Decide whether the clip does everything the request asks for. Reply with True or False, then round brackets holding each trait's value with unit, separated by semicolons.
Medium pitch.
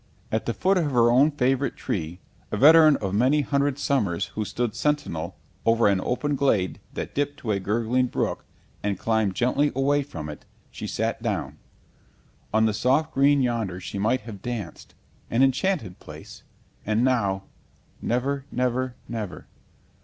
False (120 Hz)